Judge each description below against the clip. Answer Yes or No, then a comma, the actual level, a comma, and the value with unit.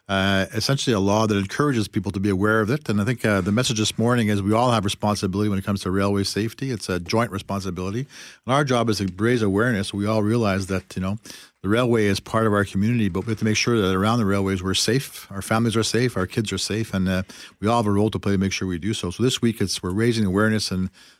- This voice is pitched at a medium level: No, low, 105 Hz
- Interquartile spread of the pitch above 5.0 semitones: No, average, 2.7 semitones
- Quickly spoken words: Yes, fast, 275 wpm